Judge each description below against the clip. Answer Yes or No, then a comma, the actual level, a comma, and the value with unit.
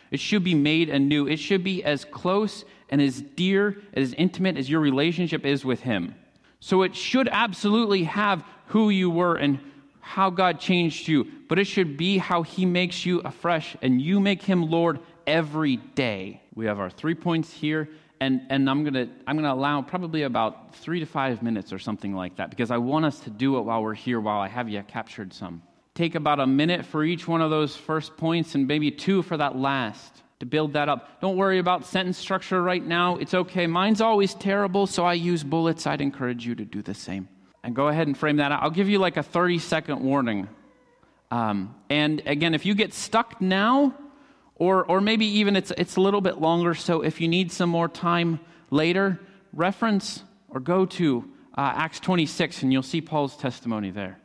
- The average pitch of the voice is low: No, medium, 165 Hz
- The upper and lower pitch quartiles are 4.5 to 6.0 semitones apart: Yes, average, 5.1 semitones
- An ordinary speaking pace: No, fast, 210 wpm